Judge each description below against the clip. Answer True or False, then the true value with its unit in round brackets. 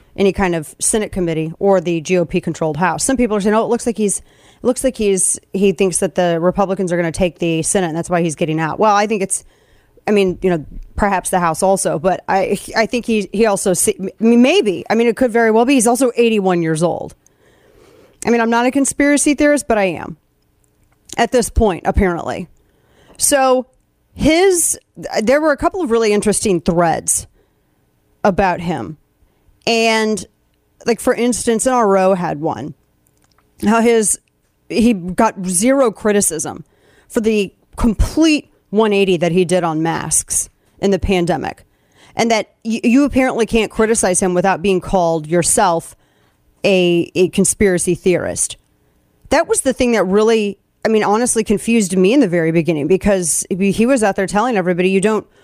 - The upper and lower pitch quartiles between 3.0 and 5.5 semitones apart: True (4.3 semitones)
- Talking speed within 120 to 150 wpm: False (180 wpm)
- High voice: True (200 Hz)